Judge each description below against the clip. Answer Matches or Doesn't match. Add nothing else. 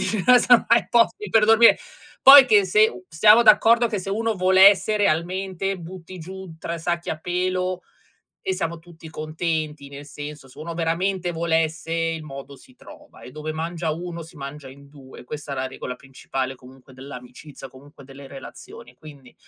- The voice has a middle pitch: Matches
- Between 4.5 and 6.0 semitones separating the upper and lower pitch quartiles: Matches